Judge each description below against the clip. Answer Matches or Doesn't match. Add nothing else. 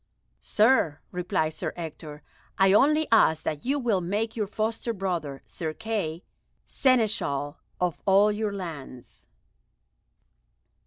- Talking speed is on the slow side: Matches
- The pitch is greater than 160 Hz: Matches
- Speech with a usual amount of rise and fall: Doesn't match